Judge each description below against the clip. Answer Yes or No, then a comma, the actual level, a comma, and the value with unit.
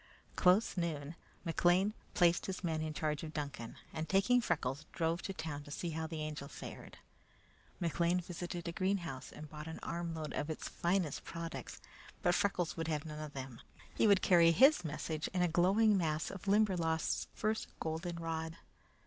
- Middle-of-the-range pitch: Yes, medium, 165 Hz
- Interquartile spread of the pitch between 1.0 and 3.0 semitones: Yes, narrow, 2.6 semitones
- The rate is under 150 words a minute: No, average, 175 wpm